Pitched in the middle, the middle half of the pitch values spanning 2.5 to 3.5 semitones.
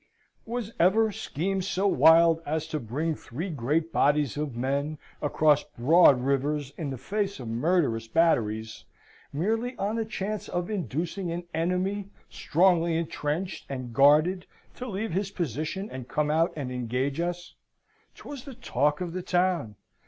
No: medium, 165 Hz; average, 5.0 semitones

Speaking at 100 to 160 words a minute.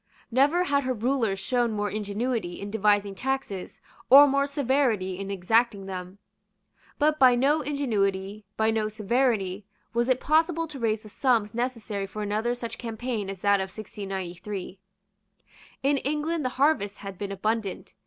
Yes: average, 155 wpm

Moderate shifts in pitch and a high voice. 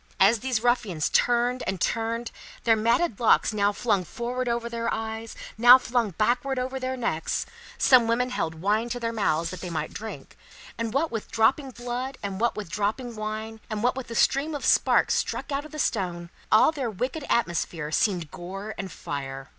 Yes: average, 3.6 semitones; high, 230 Hz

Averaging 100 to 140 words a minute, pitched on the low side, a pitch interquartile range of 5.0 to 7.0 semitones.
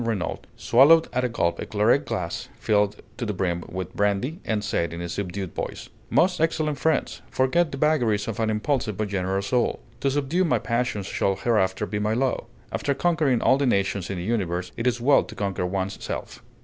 No: average, 200 wpm; low, 110 Hz; wide, 5.6 semitones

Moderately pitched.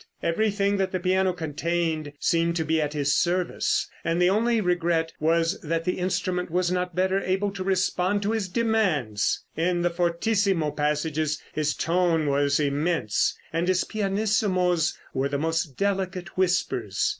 Yes: medium, 175 Hz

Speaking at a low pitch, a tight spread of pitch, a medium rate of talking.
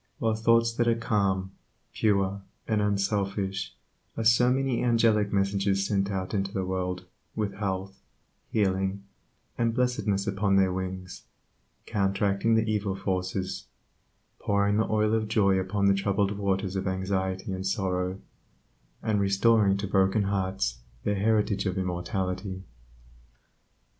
No: low, 100 Hz; narrow, 1.9 semitones; slow, 130 wpm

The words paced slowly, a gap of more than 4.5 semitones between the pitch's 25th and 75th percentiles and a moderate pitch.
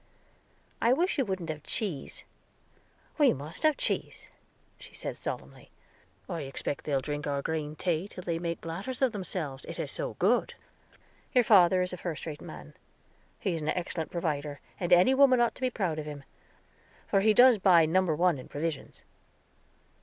No: average, 175 wpm; average, 5.2 semitones; medium, 170 Hz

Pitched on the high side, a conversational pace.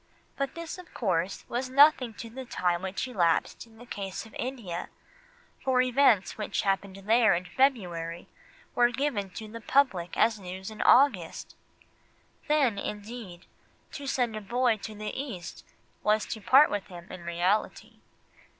Yes: high, 220 Hz; average, 160 wpm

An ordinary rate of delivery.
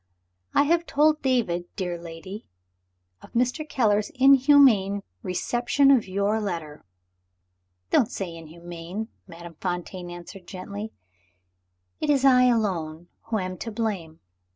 No: slow, 120 wpm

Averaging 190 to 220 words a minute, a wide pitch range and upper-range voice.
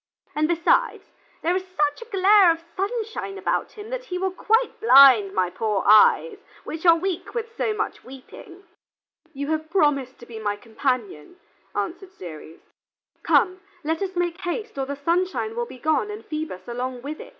No: average, 175 wpm; wide, 6.8 semitones; very high, 335 Hz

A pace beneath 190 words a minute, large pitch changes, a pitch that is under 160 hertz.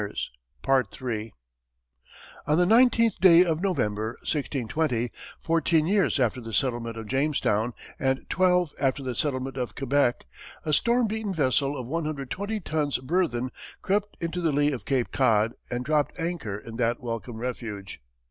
Yes: average, 140 wpm; wide, 6.0 semitones; low, 135 Hz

